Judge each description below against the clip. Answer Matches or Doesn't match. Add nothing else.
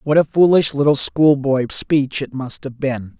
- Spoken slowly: Doesn't match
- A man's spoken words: Matches